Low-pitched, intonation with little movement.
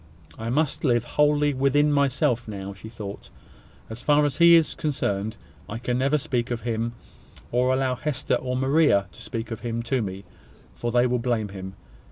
No: low, 125 Hz; average, 3.8 semitones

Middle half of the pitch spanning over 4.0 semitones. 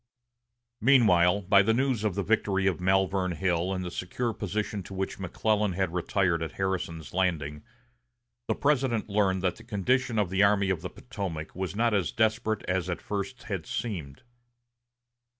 No: average, 3.0 semitones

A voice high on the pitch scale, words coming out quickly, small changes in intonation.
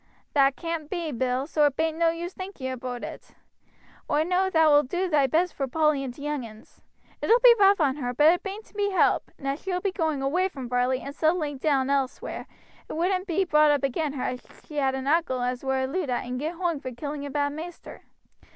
No: very high, 295 Hz; fast, 235 wpm; average, 4.3 semitones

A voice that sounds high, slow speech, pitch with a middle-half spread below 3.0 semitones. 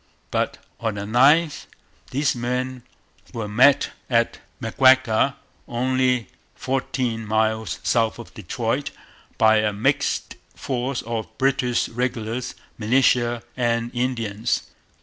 No: low, 120 Hz; slow, 105 wpm; narrow, 2.6 semitones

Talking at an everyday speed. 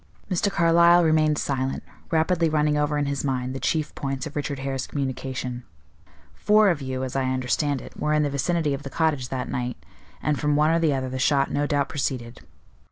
No: fast, 210 wpm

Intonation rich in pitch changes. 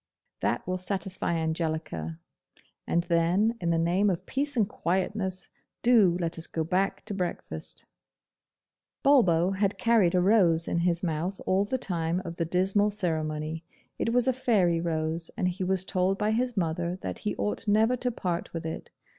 No: average, 3.6 semitones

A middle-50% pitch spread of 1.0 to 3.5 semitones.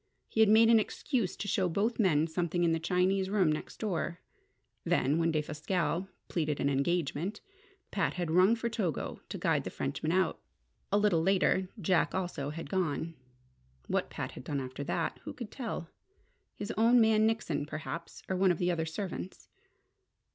No: average, 4.2 semitones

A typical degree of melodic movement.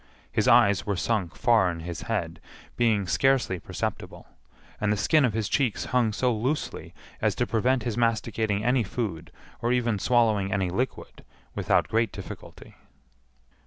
Yes: average, 3.5 semitones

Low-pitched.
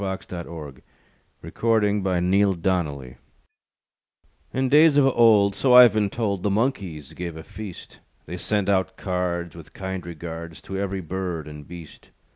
Yes: very low, 95 Hz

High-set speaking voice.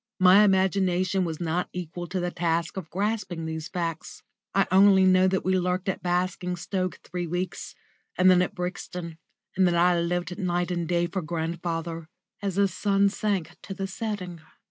No: medium, 180 Hz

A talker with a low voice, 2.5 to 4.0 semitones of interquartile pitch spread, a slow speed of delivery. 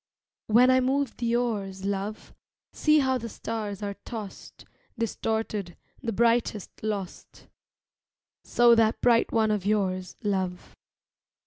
No: high, 220 Hz; average, 2.9 semitones; slow, 120 wpm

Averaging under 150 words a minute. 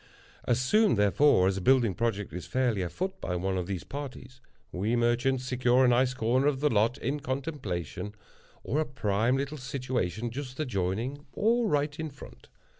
No: average, 175 wpm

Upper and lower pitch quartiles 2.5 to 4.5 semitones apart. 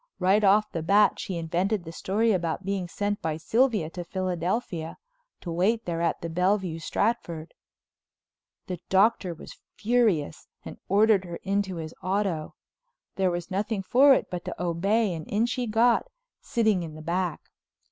Yes: average, 4.0 semitones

